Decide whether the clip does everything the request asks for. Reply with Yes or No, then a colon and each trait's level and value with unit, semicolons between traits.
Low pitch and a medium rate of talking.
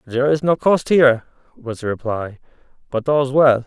Yes: low, 130 Hz; average, 180 wpm